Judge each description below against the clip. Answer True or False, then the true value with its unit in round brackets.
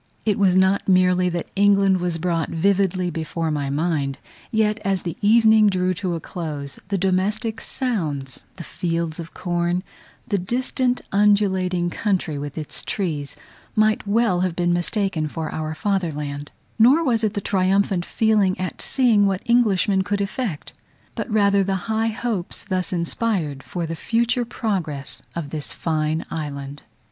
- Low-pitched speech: False (185 Hz)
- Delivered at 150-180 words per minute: True (155 wpm)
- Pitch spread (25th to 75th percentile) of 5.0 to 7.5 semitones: False (4.0 semitones)